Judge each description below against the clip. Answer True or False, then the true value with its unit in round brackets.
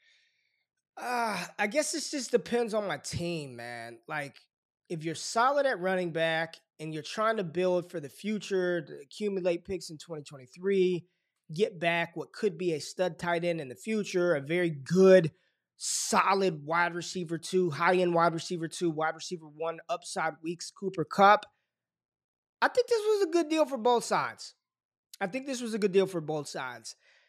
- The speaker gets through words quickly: False (180 wpm)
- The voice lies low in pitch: False (180 Hz)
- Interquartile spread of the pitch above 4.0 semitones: True (4.4 semitones)